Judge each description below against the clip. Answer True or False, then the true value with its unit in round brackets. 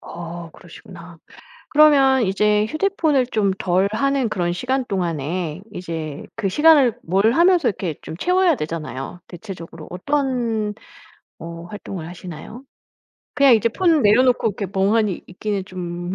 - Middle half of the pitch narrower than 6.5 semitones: False (6.8 semitones)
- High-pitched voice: True (200 Hz)